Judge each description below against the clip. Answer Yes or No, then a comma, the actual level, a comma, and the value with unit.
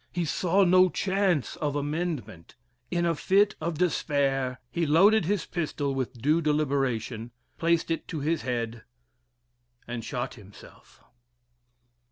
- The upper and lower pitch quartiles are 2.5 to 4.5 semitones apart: No, average, 5.1 semitones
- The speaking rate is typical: No, slow, 130 wpm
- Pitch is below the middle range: No, medium, 150 Hz